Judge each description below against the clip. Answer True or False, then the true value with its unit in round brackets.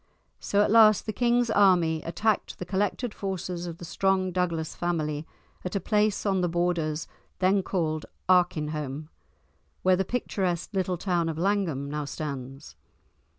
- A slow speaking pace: False (150 wpm)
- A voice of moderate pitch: True (180 Hz)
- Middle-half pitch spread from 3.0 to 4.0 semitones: True (3.6 semitones)